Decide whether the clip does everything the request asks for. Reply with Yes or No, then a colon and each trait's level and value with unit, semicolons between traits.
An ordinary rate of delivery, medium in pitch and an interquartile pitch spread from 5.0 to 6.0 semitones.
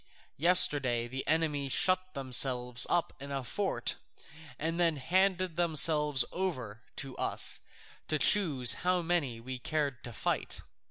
No: slow, 130 wpm; medium, 145 Hz; average, 5.3 semitones